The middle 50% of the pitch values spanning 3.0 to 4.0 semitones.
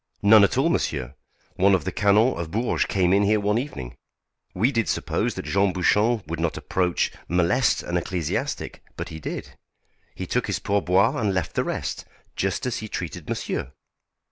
Yes: average, 3.7 semitones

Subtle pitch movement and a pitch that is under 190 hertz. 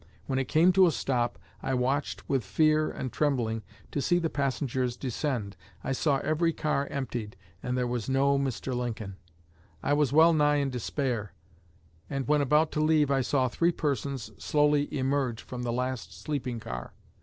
No: average, 3.2 semitones; low, 135 Hz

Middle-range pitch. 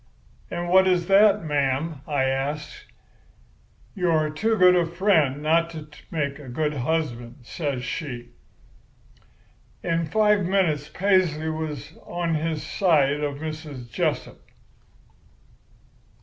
Yes: medium, 155 Hz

